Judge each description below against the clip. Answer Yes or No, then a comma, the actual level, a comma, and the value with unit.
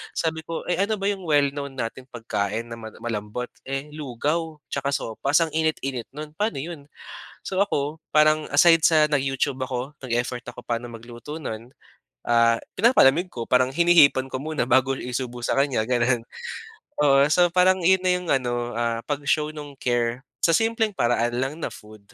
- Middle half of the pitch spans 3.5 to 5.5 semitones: Yes, average, 4.6 semitones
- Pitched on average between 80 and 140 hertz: Yes, low, 135 Hz